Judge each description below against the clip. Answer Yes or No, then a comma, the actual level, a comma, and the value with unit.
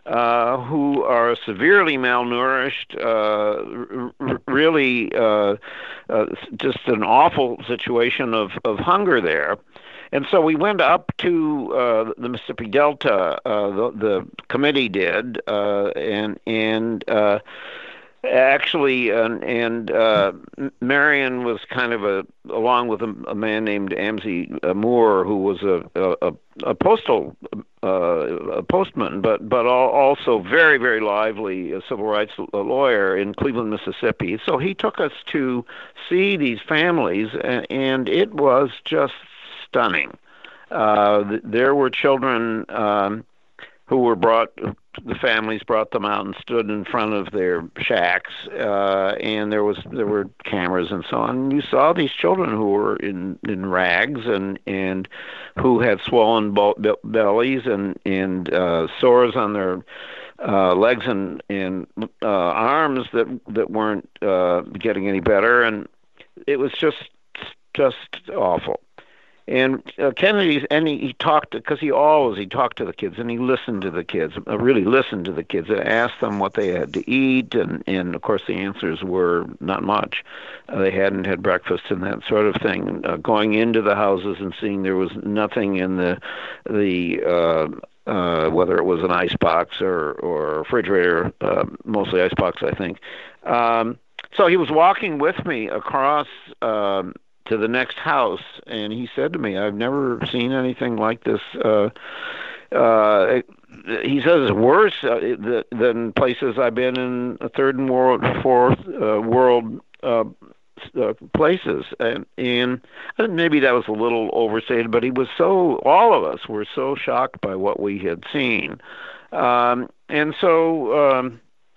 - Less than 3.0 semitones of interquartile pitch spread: No, average, 4.2 semitones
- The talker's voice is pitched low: Yes, low, 115 Hz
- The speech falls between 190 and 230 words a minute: No, average, 155 wpm